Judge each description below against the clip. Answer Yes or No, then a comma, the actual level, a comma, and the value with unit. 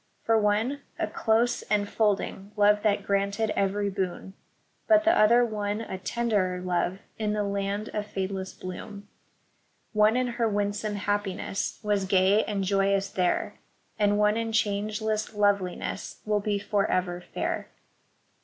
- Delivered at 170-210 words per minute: No, average, 140 wpm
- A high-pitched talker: Yes, high, 205 Hz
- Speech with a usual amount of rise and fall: No, narrow, 1.5 semitones